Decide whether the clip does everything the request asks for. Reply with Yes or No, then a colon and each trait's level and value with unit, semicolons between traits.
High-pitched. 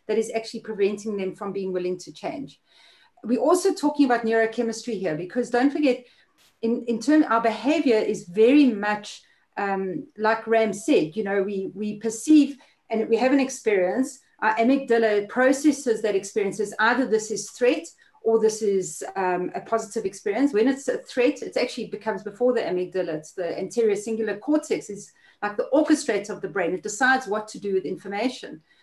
Yes: high, 225 Hz